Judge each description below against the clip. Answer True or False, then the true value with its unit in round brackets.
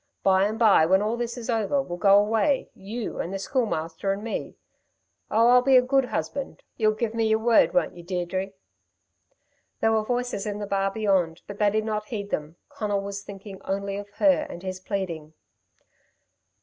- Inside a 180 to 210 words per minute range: True (190 wpm)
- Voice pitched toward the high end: True (205 Hz)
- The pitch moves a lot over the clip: False (2.8 semitones)